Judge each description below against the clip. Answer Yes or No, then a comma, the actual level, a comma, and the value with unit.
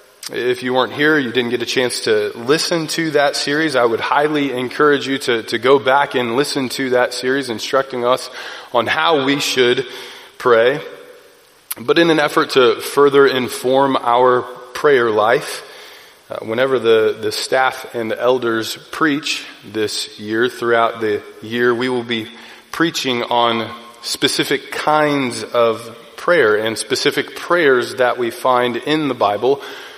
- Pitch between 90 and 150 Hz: Yes, low, 135 Hz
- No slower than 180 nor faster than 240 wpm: No, average, 155 wpm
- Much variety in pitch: Yes, wide, 6.1 semitones